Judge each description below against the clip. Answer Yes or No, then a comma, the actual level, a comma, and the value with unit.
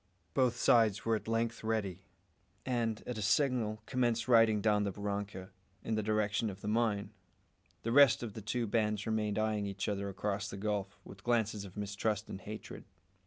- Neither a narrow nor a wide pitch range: No, narrow, 2.0 semitones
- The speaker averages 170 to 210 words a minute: Yes, average, 180 wpm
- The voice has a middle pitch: No, low, 105 Hz